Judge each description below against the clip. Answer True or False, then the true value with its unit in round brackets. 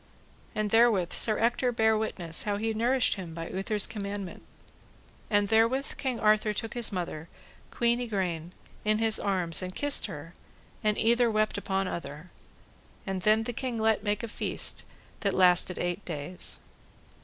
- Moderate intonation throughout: True (3.7 semitones)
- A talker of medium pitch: False (210 Hz)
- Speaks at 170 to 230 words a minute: False (155 wpm)